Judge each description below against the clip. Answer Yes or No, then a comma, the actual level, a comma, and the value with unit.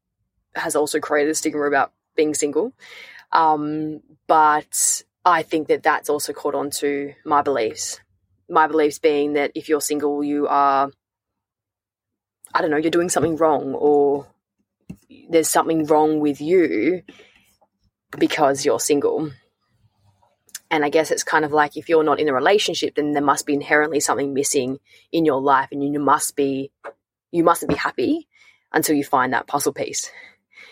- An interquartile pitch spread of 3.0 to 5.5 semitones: No, narrow, 2.4 semitones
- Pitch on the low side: No, medium, 150 Hz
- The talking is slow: No, average, 160 wpm